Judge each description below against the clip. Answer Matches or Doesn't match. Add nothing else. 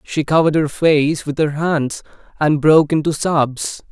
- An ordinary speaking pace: Matches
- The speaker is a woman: Doesn't match